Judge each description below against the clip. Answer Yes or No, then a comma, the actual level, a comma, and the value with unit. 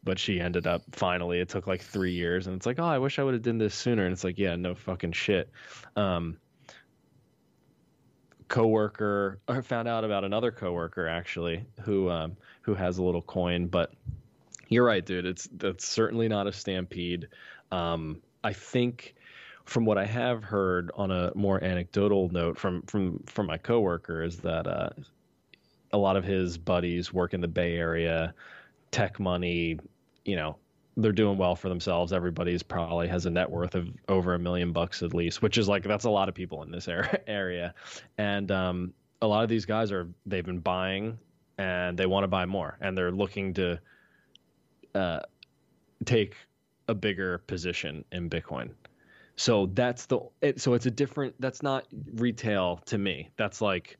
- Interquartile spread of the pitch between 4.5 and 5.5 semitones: No, average, 3.2 semitones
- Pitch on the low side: Yes, very low, 95 Hz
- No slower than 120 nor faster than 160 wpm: No, average, 180 wpm